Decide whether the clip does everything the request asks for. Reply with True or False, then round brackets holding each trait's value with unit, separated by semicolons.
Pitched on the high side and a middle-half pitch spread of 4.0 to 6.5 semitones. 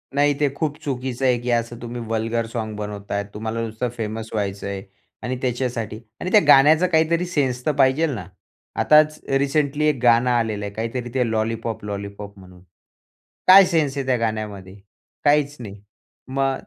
False (120 Hz; 4.6 semitones)